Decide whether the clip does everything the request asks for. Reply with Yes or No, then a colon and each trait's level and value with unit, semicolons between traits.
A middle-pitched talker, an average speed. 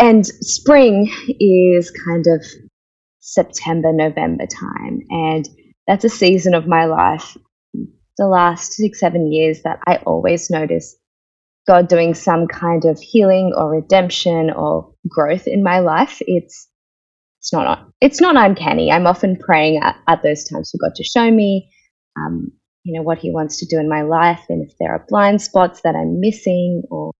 Yes: medium, 170 Hz; average, 170 wpm